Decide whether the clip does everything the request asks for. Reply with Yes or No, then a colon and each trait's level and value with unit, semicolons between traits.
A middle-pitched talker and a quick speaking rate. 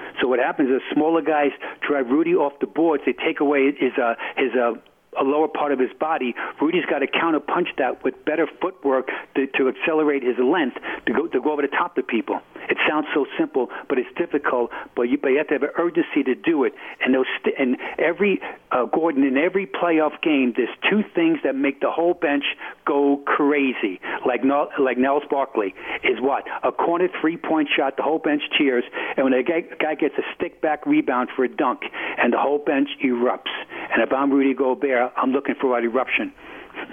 Yes: medium, 150 Hz; fast, 210 wpm